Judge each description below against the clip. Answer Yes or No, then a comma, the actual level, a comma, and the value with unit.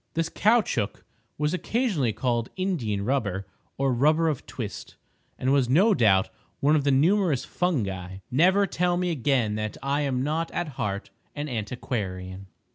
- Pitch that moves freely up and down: Yes, wide, 7.2 semitones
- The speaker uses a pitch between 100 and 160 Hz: Yes, low, 135 Hz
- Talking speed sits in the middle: Yes, average, 150 wpm